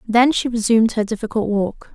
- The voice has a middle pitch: No, high, 225 Hz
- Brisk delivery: No, average, 185 wpm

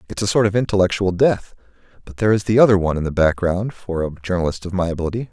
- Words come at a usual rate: No, fast, 235 wpm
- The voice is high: No, very low, 95 Hz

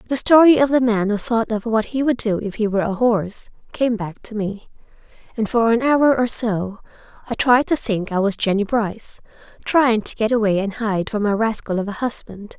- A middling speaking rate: No, fast, 225 wpm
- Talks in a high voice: Yes, high, 225 Hz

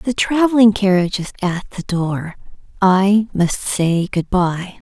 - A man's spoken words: No, female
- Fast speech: No, average, 145 wpm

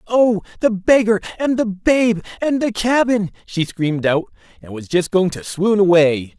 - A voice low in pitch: No, high, 195 Hz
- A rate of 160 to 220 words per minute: Yes, average, 180 wpm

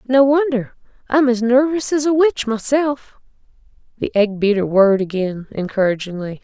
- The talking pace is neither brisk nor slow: No, slow, 130 wpm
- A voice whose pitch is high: Yes, high, 235 Hz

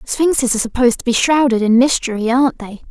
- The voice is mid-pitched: No, high, 245 Hz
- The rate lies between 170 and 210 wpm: Yes, fast, 205 wpm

